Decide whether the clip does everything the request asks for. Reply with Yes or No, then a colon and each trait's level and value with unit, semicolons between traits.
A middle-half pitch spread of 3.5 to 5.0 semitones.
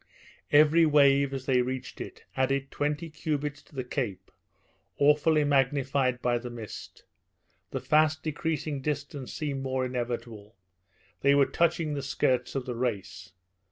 No: average, 3.0 semitones